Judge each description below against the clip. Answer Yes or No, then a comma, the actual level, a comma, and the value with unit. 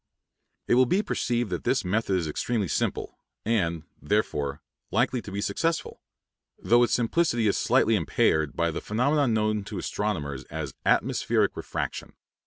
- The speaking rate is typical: Yes, average, 150 wpm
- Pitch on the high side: No, low, 105 Hz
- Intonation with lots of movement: Yes, wide, 6.1 semitones